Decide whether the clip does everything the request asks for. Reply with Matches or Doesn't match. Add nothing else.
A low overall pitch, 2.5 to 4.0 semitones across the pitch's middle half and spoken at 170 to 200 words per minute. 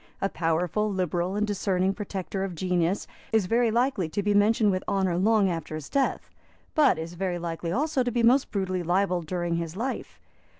Doesn't match